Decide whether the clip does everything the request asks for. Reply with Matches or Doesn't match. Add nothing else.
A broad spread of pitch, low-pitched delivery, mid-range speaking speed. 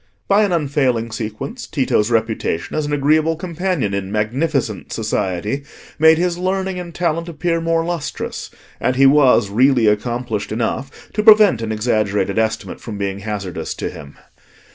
Matches